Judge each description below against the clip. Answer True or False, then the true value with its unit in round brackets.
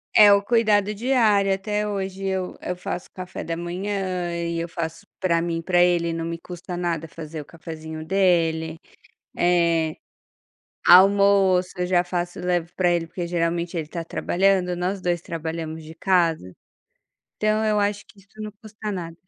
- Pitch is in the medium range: True (180 Hz)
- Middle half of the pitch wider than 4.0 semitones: False (2.8 semitones)